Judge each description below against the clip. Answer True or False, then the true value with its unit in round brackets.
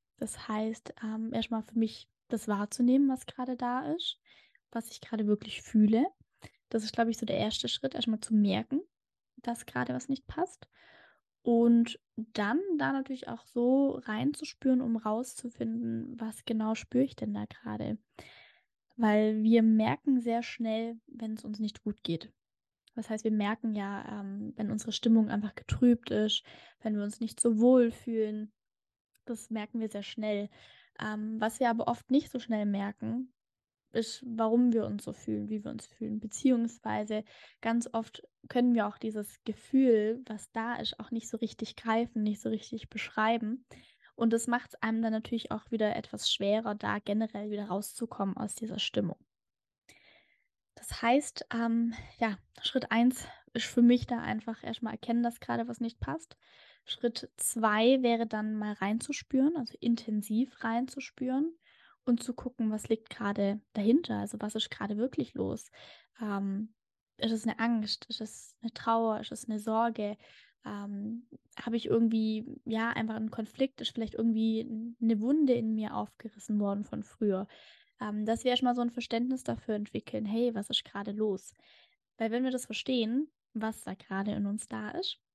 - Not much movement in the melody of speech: True (2.1 semitones)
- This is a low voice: False (225 Hz)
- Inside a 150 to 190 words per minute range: True (170 wpm)